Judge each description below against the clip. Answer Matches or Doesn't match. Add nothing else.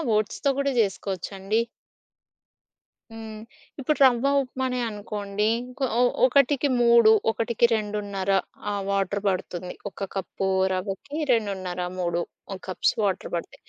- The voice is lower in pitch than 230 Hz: Matches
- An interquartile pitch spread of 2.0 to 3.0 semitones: Doesn't match